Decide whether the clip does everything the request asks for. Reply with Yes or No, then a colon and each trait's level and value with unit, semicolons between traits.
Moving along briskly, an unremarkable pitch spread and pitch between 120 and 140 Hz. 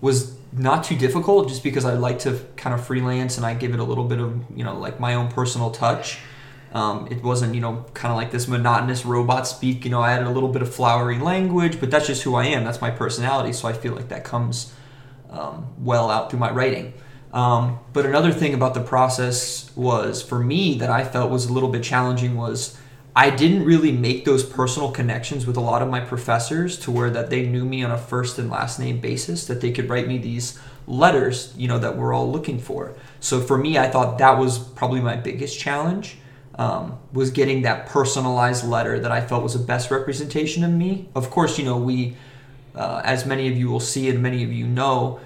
No: fast, 230 wpm; narrow, 1.6 semitones; low, 125 Hz